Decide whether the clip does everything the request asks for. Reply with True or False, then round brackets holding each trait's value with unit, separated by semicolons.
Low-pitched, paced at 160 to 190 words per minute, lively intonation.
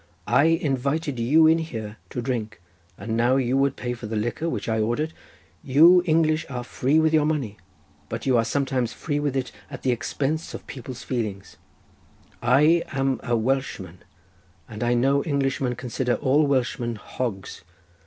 False (130 Hz; 165 wpm; 3.6 semitones)